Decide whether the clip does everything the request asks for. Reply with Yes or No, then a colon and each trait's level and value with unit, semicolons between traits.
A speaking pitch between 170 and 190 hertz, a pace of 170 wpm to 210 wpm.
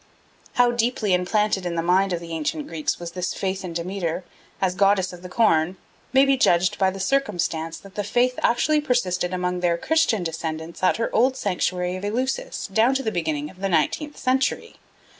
Yes: medium, 185 Hz; average, 195 wpm